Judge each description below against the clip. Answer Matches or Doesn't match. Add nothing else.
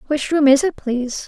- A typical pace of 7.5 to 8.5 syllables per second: Doesn't match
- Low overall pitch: Doesn't match